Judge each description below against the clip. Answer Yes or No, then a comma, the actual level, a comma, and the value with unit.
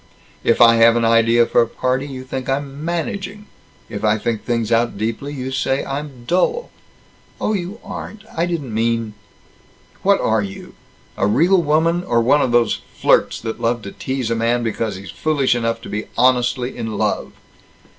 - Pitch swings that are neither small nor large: Yes, average, 4.2 semitones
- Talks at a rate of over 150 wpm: Yes, average, 185 wpm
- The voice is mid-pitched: No, low, 120 Hz